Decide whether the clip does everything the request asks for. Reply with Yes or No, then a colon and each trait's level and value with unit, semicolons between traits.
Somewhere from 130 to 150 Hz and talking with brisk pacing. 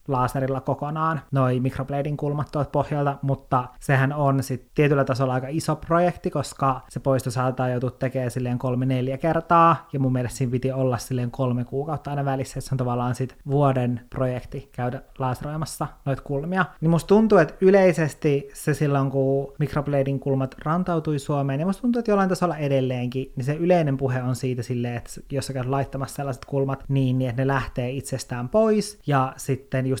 Yes: low, 135 Hz; fast, 180 wpm